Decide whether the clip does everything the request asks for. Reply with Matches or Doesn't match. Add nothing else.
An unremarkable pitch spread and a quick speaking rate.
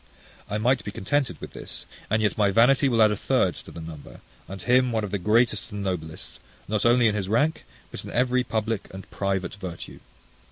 Matches